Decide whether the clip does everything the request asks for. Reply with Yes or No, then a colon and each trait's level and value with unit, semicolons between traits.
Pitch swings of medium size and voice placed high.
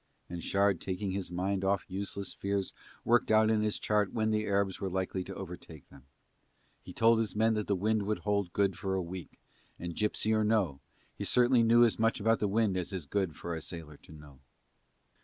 No: average, 3.0 semitones; low, 100 Hz